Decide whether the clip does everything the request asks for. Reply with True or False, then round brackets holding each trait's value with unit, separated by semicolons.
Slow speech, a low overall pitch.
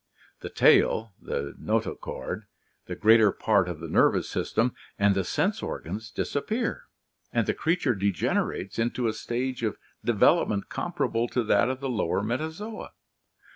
False (145 wpm; 115 Hz)